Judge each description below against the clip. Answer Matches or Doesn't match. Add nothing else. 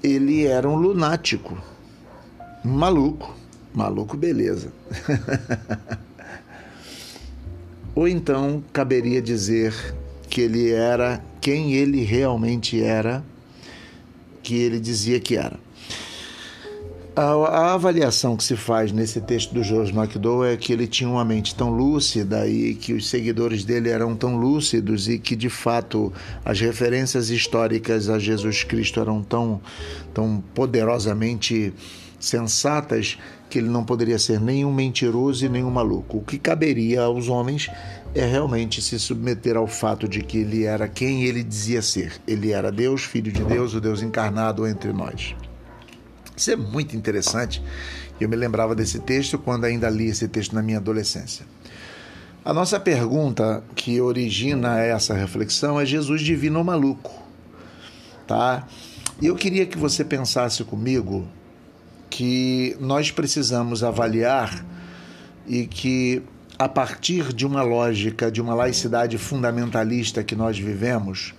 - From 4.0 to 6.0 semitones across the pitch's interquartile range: Doesn't match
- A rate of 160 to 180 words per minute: Doesn't match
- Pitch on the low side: Matches